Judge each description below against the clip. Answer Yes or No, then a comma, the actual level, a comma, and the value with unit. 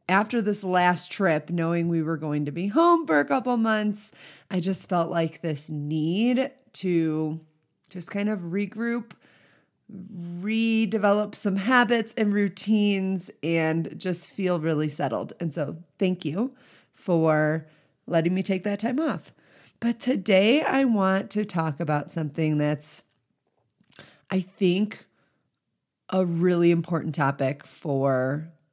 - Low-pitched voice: No, medium, 180 Hz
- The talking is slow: Yes, slow, 130 wpm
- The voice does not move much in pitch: No, average, 4.8 semitones